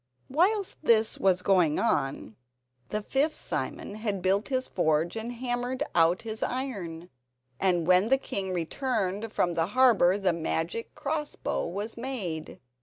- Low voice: No, high, 205 Hz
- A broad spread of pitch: Yes, wide, 6.3 semitones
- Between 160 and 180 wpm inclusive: No, average, 145 wpm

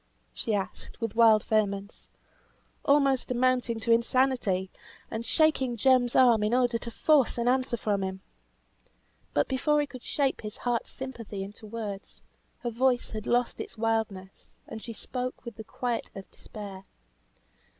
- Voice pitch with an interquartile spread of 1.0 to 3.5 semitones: Yes, average, 3.2 semitones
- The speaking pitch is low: No, high, 230 Hz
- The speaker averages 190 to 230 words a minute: No, average, 150 wpm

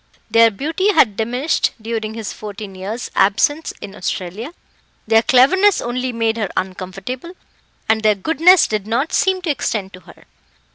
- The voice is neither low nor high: No, high, 225 Hz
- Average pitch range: No, wide, 5.9 semitones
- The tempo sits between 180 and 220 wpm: No, average, 150 wpm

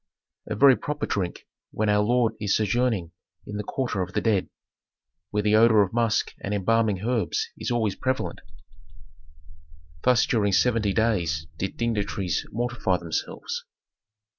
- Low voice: Yes, low, 105 Hz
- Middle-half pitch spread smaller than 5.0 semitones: Yes, average, 3.2 semitones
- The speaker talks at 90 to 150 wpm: Yes, average, 140 wpm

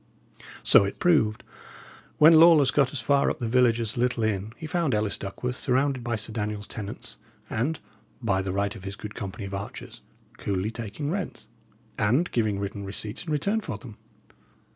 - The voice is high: No, low, 115 Hz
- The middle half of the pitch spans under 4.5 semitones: No, wide, 5.6 semitones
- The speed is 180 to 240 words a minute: Yes, average, 185 wpm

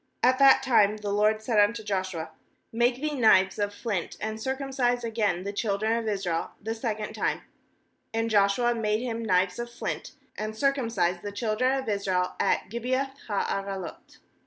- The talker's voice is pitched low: No, high, 220 Hz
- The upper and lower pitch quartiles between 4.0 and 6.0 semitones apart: No, average, 3.2 semitones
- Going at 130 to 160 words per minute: No, average, 170 wpm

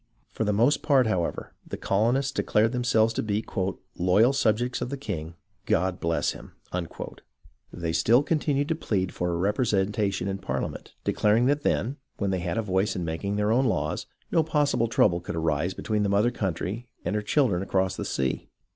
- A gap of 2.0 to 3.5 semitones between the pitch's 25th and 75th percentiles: No, average, 4.8 semitones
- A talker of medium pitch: No, low, 105 Hz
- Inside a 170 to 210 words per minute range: Yes, average, 185 wpm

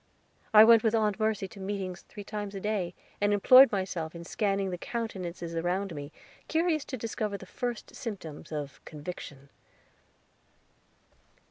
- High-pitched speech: Yes, high, 200 Hz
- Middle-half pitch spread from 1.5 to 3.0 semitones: No, average, 3.8 semitones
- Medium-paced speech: Yes, average, 145 wpm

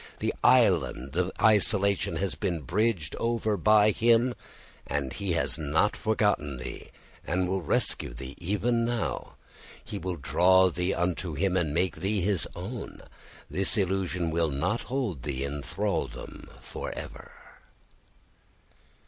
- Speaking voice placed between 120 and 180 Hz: No, very low, 90 Hz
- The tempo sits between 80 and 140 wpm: Yes, slow, 135 wpm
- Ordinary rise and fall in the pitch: Yes, average, 4.6 semitones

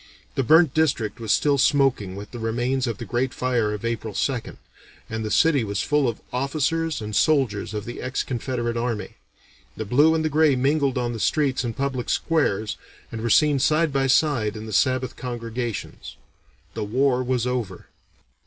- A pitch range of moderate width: Yes, average, 3.8 semitones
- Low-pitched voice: Yes, low, 125 Hz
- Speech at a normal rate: Yes, average, 180 wpm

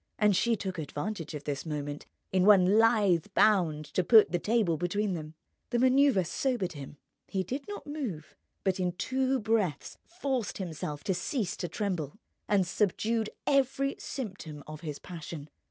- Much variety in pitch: Yes, wide, 5.9 semitones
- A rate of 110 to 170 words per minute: Yes, average, 160 wpm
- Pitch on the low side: No, high, 190 Hz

